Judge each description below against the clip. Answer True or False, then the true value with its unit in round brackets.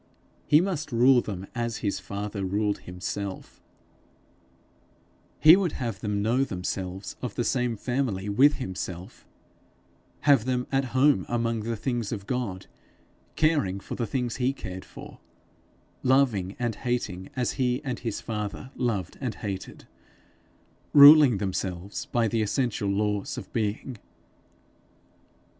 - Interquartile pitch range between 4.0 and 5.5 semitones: True (4.4 semitones)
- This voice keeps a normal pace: False (130 wpm)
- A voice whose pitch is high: False (115 Hz)